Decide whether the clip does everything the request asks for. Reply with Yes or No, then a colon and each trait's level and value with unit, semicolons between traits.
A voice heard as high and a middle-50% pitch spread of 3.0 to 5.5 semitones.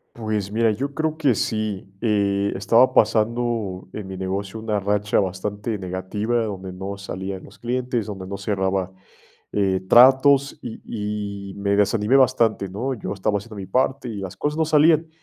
No: low, 105 Hz; average, 3.4 semitones